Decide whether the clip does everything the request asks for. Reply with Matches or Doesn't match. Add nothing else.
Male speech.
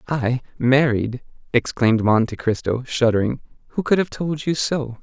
Matches